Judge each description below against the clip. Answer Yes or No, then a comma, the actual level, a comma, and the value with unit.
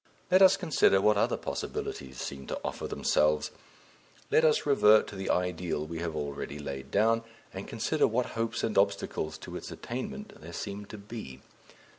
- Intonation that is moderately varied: No, wide, 7.0 semitones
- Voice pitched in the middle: No, low, 100 Hz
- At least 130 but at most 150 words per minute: No, average, 170 wpm